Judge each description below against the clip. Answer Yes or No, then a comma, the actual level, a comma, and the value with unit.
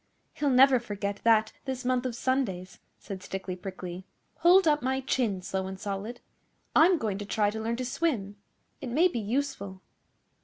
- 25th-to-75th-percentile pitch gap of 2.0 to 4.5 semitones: No, average, 5.2 semitones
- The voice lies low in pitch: No, high, 225 Hz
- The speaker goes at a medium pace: Yes, average, 175 wpm